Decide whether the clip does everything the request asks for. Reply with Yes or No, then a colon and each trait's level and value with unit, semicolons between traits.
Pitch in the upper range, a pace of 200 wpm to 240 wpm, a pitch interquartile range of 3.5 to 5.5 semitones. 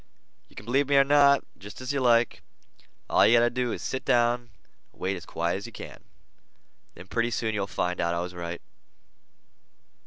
No: low, 115 Hz; fast, 205 wpm; average, 5.2 semitones